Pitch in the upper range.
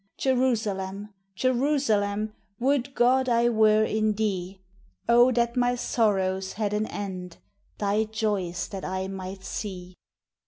Yes: high, 215 Hz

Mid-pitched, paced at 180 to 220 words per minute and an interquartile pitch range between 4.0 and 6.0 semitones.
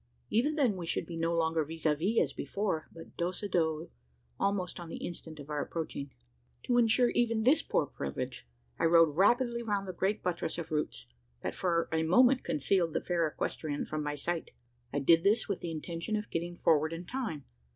Yes: medium, 170 Hz; fast, 205 wpm; average, 4.3 semitones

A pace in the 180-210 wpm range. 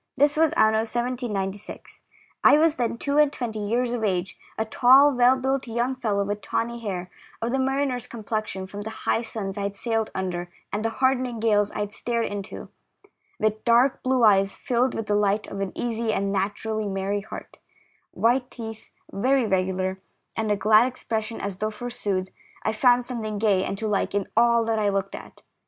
Yes: average, 190 wpm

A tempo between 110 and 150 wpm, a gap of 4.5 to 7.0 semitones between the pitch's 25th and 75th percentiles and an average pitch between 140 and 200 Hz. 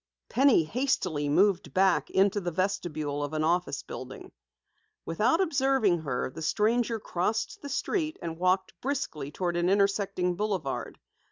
Yes: average, 140 wpm; wide, 5.4 semitones; medium, 185 Hz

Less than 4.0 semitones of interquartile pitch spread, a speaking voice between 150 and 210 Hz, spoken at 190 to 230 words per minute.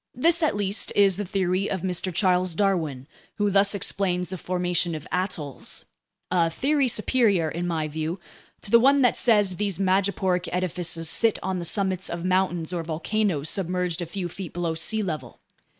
No: average, 2.8 semitones; medium, 185 Hz; average, 170 wpm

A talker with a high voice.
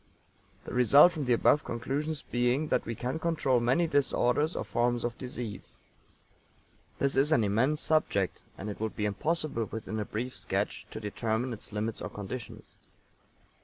No: low, 125 Hz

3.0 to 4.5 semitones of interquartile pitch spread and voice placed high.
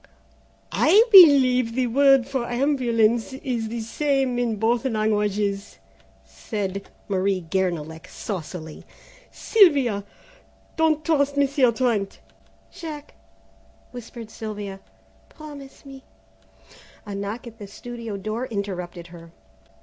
No: average, 5.1 semitones; high, 230 Hz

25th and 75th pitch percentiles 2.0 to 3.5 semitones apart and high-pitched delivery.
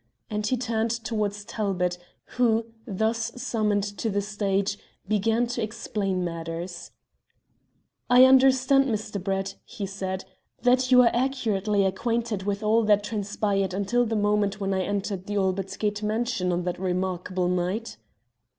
Yes: average, 2.9 semitones; high, 205 Hz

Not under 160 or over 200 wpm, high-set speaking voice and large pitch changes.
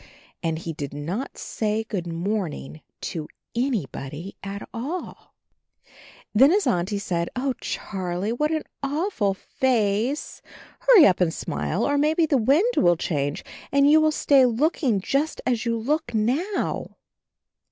No: average, 140 wpm; high, 225 Hz; wide, 8.3 semitones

